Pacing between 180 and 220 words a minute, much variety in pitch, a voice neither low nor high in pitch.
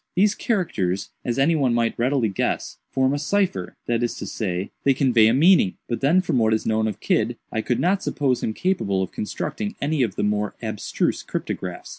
No: average, 200 wpm; wide, 6.0 semitones; low, 120 Hz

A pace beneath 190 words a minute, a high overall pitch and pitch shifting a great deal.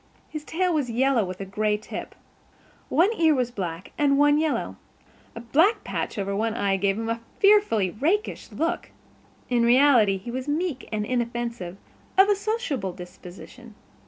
Yes: average, 160 wpm; high, 240 Hz; wide, 6.7 semitones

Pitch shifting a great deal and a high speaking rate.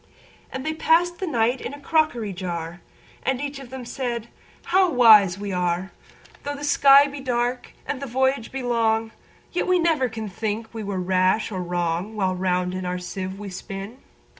No: wide, 6.4 semitones; average, 170 wpm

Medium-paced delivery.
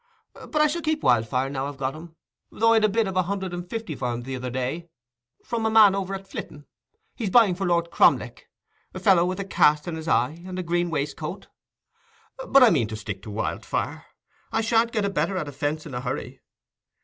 No: fast, 220 wpm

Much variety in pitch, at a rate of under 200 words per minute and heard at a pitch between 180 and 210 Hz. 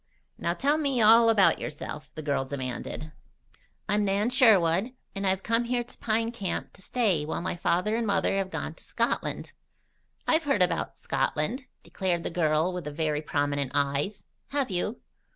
Yes: wide, 6.6 semitones; average, 170 wpm; high, 190 Hz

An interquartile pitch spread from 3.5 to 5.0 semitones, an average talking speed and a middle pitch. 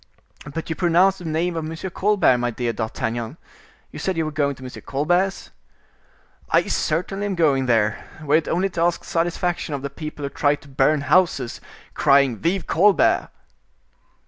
Yes: average, 4.2 semitones; average, 175 wpm; medium, 155 Hz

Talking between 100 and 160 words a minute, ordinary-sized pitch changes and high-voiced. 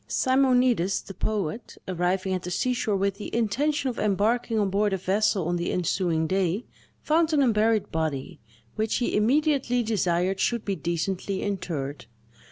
Yes: average, 155 wpm; average, 4.6 semitones; high, 200 Hz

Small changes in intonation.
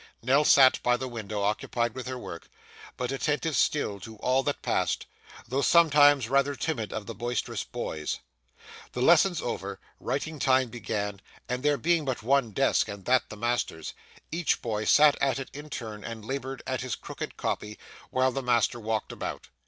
No: average, 4.0 semitones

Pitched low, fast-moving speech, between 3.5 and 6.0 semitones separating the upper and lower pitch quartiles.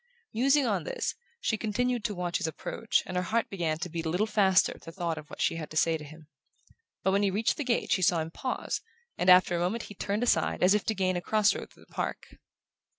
No: high, 190 Hz; fast, 260 wpm; average, 4.5 semitones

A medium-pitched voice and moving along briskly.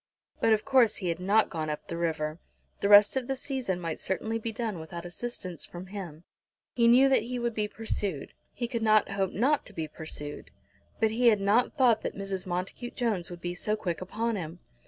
No: high, 205 Hz; fast, 215 wpm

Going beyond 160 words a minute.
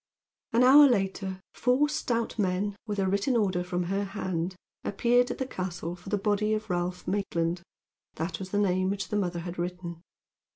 Yes: average, 180 wpm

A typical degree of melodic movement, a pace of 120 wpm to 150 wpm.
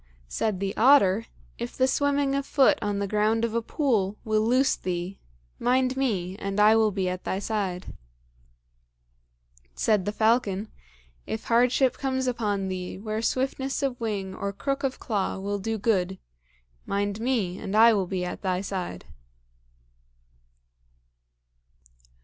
Yes: average, 4.4 semitones; average, 145 wpm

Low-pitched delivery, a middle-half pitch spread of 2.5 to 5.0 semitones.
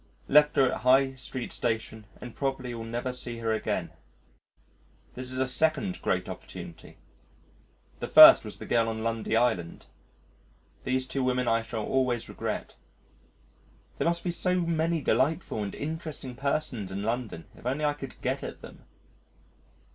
Yes: low, 125 Hz; average, 3.6 semitones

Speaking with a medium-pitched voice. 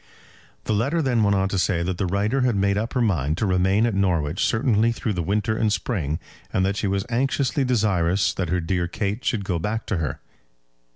No: low, 100 Hz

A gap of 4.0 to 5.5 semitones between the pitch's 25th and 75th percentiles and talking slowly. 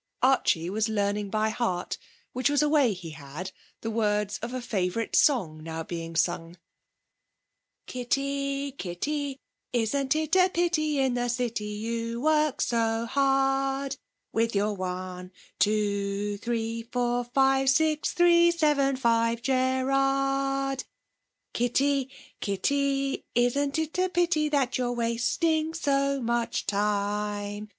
Yes: average, 4.9 semitones; slow, 125 wpm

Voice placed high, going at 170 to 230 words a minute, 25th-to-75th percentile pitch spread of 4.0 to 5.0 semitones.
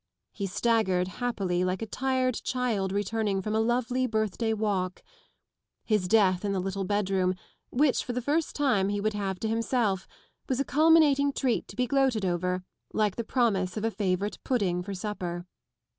Yes: high, 210 Hz; average, 175 wpm; average, 4.5 semitones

